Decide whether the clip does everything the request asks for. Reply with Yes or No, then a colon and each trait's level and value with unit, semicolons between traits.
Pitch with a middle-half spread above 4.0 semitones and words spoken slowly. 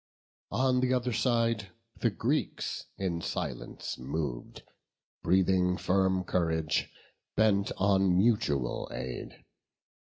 Yes: average, 4.6 semitones; slow, 95 wpm